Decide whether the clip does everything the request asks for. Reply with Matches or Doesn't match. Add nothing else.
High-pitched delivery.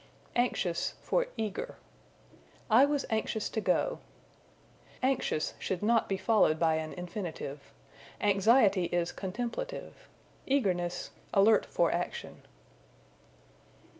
Matches